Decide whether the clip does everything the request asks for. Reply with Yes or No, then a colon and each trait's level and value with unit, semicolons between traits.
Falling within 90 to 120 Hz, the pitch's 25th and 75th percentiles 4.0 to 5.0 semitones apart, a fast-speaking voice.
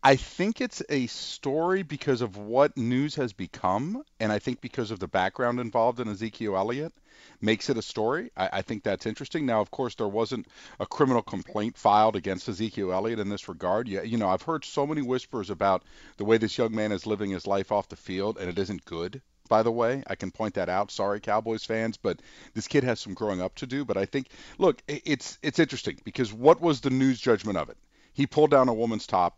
Yes: low, 115 Hz; average, 4.5 semitones; fast, 230 wpm